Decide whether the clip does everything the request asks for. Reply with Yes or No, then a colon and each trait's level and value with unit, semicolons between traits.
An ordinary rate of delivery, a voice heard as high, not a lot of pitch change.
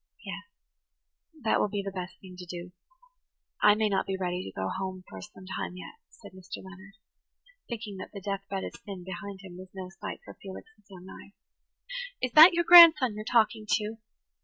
Yes: average, 195 wpm; high, 195 Hz; narrow, 2.3 semitones